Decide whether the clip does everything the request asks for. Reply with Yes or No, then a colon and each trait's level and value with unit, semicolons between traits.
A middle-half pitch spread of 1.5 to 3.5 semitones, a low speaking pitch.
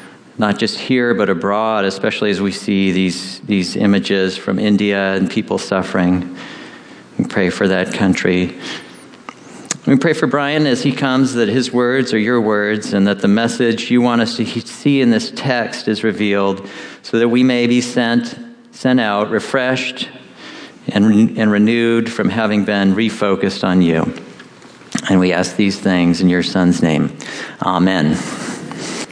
No: average, 4.1 semitones; low, 105 Hz